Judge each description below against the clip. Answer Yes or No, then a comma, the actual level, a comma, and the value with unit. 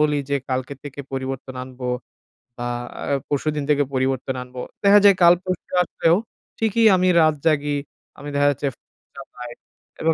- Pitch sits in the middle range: Yes, medium, 145 Hz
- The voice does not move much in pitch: No, average, 3.5 semitones